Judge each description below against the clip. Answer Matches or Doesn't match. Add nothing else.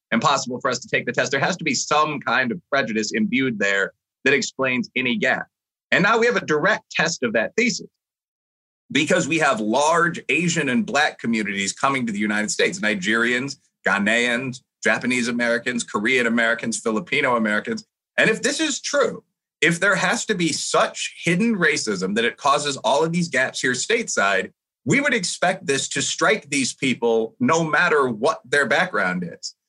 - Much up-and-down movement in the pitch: Matches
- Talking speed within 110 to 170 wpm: Doesn't match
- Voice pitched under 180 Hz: Matches